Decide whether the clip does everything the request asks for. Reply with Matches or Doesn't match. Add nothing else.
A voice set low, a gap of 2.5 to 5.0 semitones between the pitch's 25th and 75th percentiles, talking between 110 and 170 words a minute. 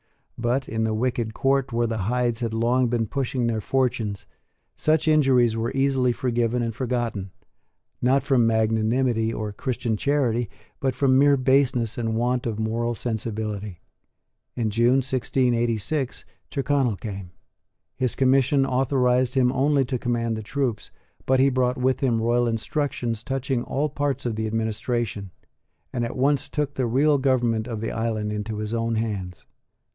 Matches